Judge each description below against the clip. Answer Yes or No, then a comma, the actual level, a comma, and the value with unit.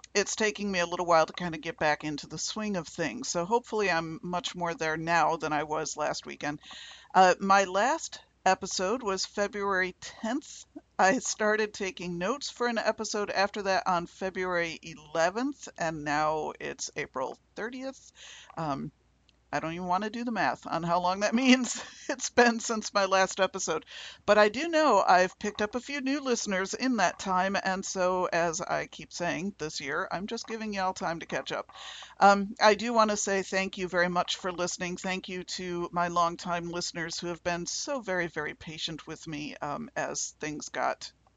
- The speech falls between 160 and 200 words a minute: Yes, average, 195 wpm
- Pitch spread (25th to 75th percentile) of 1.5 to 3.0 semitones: No, average, 3.7 semitones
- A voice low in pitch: No, medium, 185 Hz